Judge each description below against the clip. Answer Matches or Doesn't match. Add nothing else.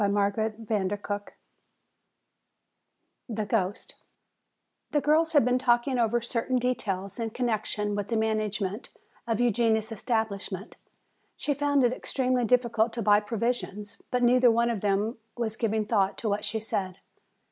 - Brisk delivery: Doesn't match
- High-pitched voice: Matches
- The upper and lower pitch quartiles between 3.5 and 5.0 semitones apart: Doesn't match